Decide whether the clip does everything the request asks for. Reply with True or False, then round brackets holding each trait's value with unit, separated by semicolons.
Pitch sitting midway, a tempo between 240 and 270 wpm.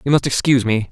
False (125 Hz; 265 wpm)